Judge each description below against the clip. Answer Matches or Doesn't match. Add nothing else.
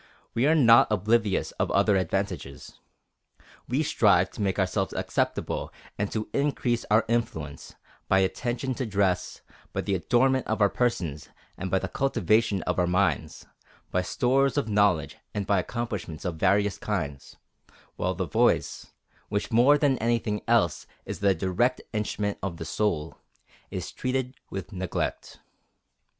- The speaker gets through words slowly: Doesn't match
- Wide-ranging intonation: Doesn't match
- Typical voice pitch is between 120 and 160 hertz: Doesn't match